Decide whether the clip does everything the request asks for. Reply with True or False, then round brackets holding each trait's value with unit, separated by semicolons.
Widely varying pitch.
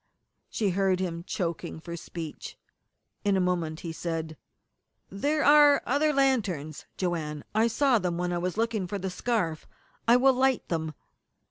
True (6.0 semitones)